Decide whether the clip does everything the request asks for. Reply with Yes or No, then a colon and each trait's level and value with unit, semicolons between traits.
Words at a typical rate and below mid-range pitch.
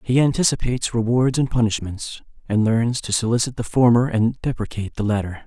Yes: average, 165 wpm; low, 115 Hz